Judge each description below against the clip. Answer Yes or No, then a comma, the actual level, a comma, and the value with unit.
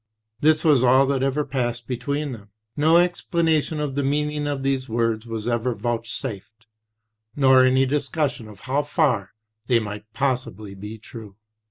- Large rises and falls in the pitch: No, average, 4.1 semitones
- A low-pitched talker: Yes, low, 130 Hz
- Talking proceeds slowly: No, average, 160 wpm